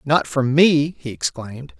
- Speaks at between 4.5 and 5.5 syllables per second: No, 4.3 syllables/s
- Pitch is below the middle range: No, medium, 145 Hz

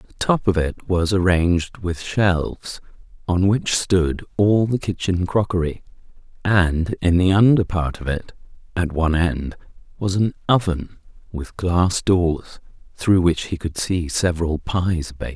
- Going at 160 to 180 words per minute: No, average, 150 wpm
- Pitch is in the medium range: No, very low, 90 Hz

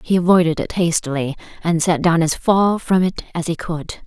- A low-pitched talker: No, medium, 170 Hz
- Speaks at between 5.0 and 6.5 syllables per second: Yes, 5.1 syllables/s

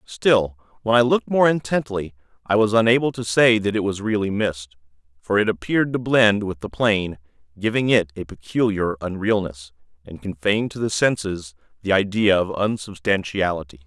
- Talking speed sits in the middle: Yes, average, 165 wpm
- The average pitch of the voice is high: No, low, 100 Hz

